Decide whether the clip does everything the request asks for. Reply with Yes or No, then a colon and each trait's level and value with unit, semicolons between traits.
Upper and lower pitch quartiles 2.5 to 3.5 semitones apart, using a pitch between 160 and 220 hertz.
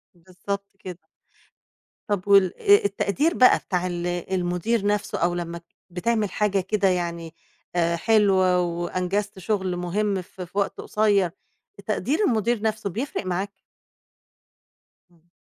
Yes: average, 2.9 semitones; high, 190 Hz